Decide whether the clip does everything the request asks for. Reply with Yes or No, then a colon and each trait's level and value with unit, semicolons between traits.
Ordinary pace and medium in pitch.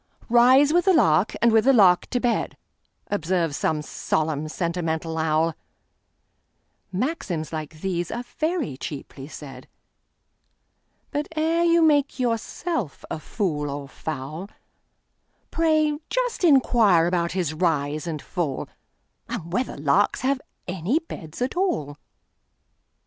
No: slow, 110 wpm; medium, 180 Hz